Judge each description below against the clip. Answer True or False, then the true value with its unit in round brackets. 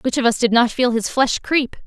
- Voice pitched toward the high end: True (245 Hz)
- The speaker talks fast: True (290 wpm)